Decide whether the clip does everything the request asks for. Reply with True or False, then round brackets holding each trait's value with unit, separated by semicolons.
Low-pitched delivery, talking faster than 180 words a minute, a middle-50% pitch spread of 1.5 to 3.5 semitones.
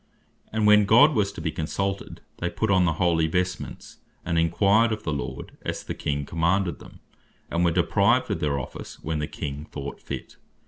False (85 Hz; 190 wpm; 3.9 semitones)